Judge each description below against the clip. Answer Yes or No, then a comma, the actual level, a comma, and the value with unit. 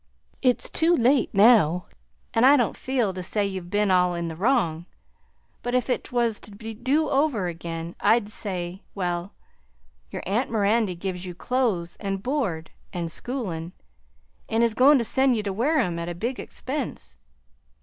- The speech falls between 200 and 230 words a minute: No, average, 165 wpm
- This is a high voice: Yes, high, 210 Hz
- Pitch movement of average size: No, wide, 5.8 semitones